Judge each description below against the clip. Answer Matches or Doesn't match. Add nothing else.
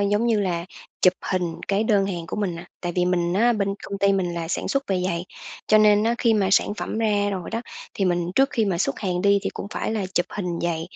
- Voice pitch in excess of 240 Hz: Doesn't match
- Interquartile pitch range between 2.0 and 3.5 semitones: Matches